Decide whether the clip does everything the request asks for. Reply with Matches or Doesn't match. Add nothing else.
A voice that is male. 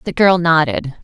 Doesn't match